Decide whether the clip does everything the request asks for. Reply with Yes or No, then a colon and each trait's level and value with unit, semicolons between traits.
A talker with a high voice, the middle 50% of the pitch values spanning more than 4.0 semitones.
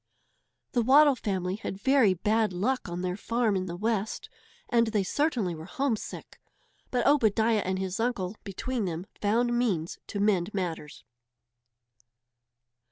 Yes: high, 210 Hz; average, 4.4 semitones